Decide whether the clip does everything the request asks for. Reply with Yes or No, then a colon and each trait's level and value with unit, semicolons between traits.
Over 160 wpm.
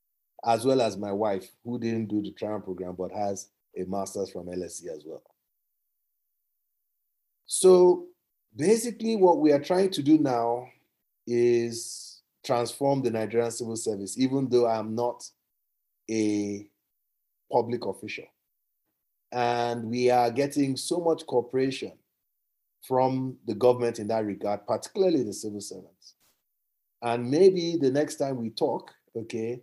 No: slow, 135 wpm